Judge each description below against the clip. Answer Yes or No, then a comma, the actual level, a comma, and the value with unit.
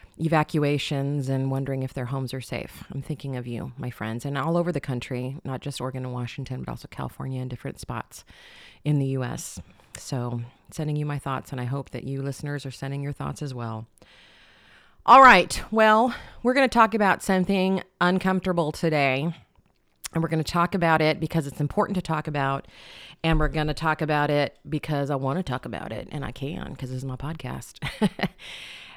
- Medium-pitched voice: Yes, medium, 145 Hz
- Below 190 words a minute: No, average, 200 wpm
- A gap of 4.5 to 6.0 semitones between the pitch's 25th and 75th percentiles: No, average, 3.5 semitones